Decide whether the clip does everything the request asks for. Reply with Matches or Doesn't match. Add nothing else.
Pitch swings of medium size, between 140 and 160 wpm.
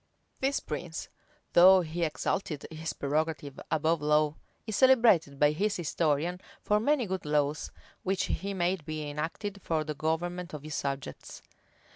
Matches